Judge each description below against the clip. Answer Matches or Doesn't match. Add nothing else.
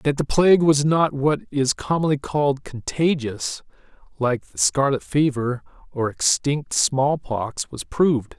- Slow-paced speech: Doesn't match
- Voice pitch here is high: Doesn't match